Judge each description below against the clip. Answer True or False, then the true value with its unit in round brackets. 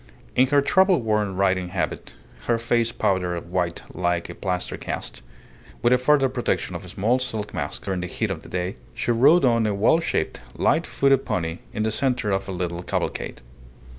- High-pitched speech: False (105 Hz)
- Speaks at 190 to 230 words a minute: True (195 wpm)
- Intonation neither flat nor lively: False (5.7 semitones)